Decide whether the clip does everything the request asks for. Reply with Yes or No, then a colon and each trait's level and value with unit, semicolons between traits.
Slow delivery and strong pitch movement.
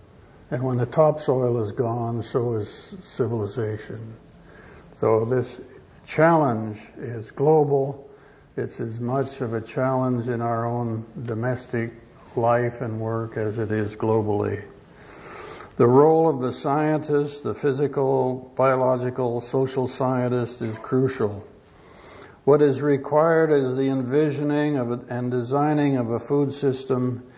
No: slow, 125 wpm; average, 3.2 semitones